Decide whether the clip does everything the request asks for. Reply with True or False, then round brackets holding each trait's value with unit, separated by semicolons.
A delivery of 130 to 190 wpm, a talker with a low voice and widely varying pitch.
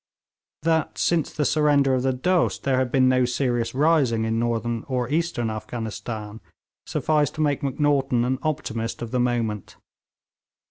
False (150 wpm; 130 Hz; 3.8 semitones)